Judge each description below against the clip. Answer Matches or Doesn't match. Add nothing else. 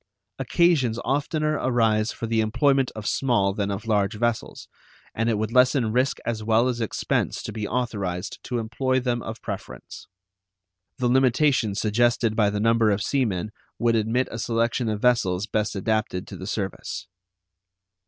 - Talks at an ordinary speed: Matches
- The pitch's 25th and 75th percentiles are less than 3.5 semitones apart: Matches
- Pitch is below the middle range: Matches